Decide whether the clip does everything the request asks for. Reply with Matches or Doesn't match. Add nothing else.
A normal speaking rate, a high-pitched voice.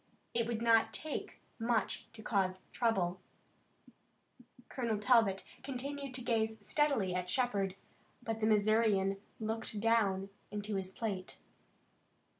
Doesn't match